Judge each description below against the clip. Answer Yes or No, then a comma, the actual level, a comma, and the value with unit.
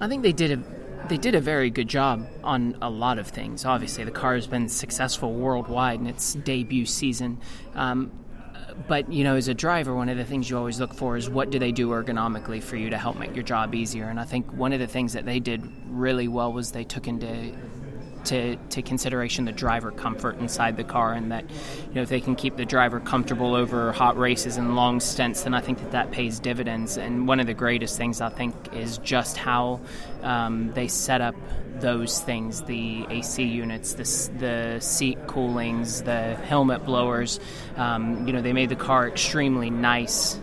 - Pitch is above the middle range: No, low, 125 Hz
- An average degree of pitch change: No, narrow, 1.6 semitones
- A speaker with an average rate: No, fast, 210 wpm